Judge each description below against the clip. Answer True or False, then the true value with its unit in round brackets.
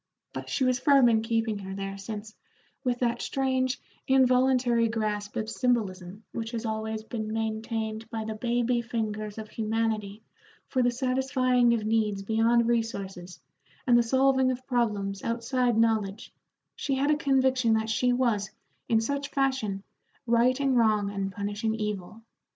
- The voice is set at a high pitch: True (225 Hz)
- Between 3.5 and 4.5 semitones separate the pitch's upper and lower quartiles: False (2.8 semitones)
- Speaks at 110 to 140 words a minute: False (150 wpm)